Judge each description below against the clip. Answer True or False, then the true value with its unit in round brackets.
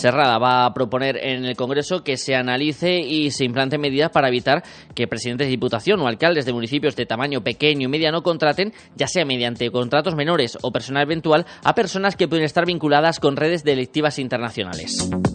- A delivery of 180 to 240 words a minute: True (190 wpm)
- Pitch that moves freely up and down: False (3.8 semitones)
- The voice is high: False (145 Hz)